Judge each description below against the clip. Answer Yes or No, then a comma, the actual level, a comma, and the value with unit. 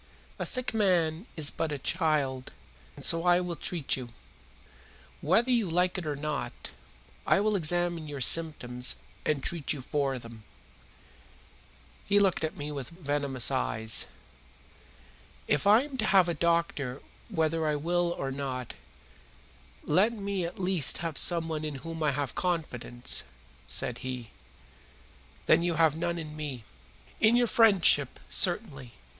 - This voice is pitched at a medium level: Yes, medium, 160 Hz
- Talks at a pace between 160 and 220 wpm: No, average, 145 wpm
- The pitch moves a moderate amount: Yes, average, 4.1 semitones